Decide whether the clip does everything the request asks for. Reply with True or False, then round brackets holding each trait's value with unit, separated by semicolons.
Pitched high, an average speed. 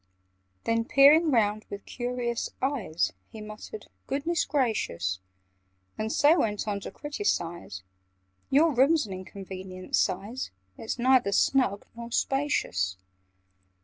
False (230 Hz; 115 wpm)